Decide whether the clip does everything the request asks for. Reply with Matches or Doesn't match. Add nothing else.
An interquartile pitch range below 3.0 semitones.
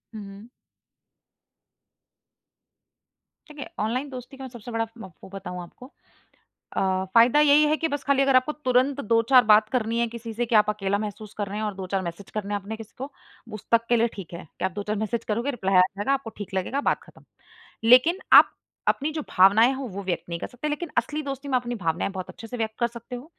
Doesn't match